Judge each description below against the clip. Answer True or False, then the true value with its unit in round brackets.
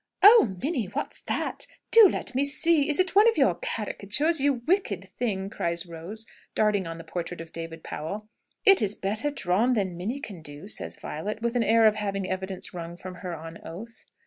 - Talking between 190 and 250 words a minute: True (195 wpm)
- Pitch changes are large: True (6.9 semitones)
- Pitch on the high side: True (205 Hz)